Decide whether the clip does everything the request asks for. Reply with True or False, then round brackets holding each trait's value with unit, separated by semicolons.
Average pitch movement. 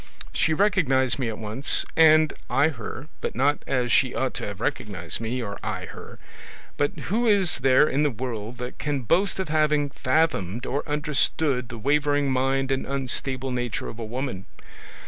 True (3.5 semitones)